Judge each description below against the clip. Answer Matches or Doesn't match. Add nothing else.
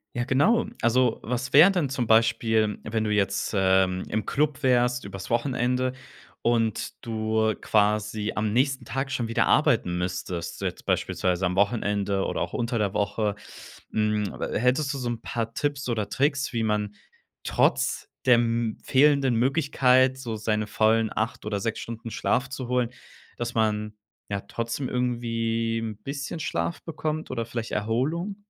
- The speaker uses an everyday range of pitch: Matches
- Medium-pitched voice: Doesn't match